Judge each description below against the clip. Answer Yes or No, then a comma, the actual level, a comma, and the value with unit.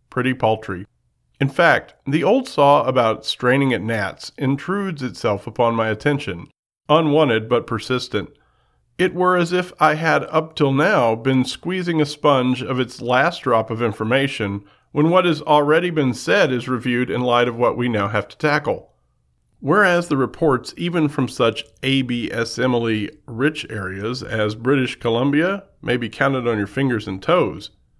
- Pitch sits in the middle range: No, low, 130 Hz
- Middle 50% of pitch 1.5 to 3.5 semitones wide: No, average, 4.8 semitones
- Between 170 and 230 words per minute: No, average, 160 wpm